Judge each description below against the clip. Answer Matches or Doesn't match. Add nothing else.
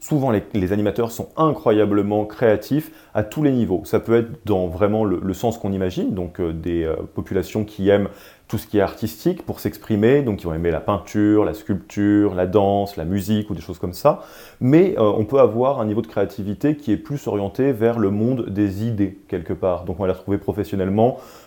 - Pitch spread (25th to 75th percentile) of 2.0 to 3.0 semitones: Matches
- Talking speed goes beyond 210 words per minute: Matches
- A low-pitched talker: Matches